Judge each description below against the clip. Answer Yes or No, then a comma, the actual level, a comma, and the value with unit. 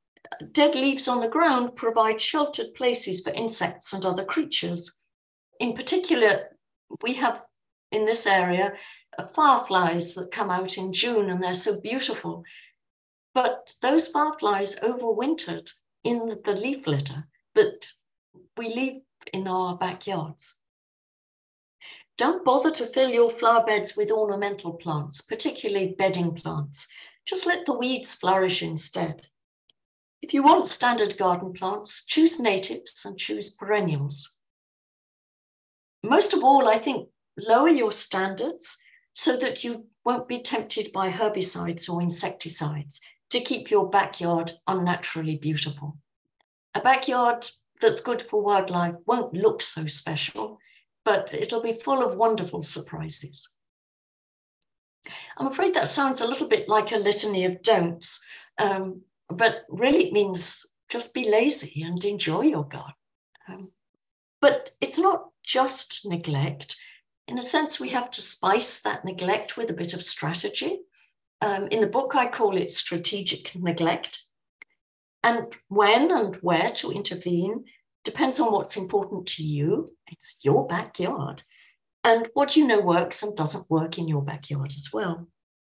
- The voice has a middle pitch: No, high, 210 Hz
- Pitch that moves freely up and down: Yes, wide, 6.2 semitones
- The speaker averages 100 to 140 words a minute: Yes, slow, 135 wpm